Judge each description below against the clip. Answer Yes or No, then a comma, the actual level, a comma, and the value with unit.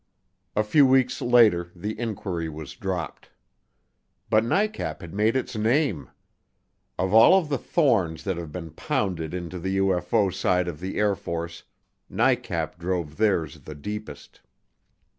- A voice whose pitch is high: No, very low, 95 Hz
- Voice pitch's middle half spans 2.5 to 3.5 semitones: No, average, 4.6 semitones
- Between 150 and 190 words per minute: No, average, 140 wpm